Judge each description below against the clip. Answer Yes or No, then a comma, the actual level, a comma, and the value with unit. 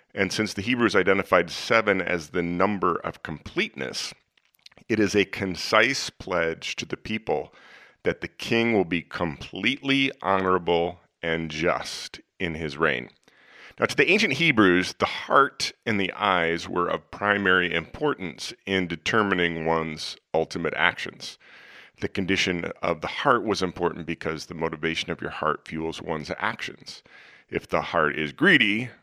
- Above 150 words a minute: No, average, 145 wpm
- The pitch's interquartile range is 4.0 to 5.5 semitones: No, average, 3.3 semitones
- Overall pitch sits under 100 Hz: Yes, very low, 90 Hz